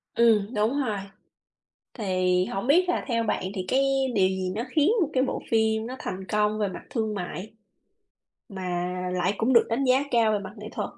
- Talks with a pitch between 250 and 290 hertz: No, high, 215 Hz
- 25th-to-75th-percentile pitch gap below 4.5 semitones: Yes, average, 3.8 semitones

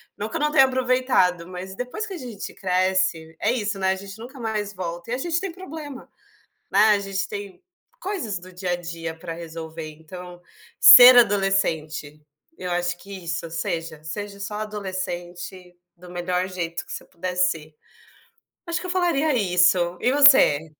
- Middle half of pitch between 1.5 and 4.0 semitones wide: No, average, 4.7 semitones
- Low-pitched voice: No, high, 190 Hz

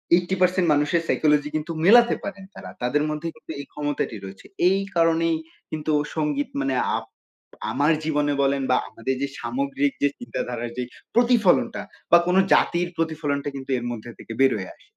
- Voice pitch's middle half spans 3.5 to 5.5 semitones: Yes, average, 4.3 semitones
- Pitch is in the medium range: Yes, medium, 150 Hz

